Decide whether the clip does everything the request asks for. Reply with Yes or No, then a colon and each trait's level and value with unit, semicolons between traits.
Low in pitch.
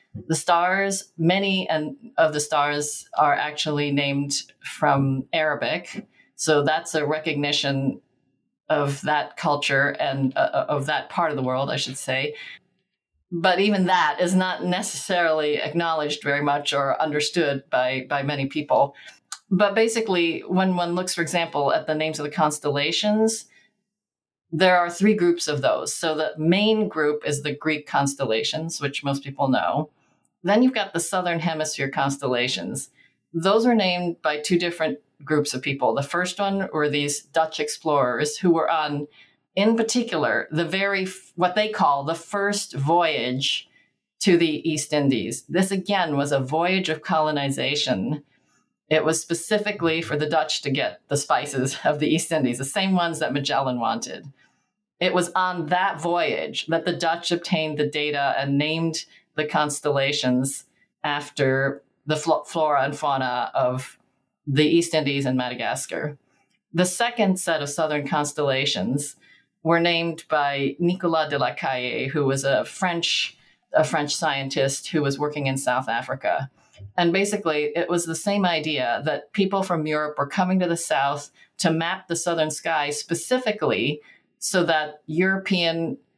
No: medium, 155 Hz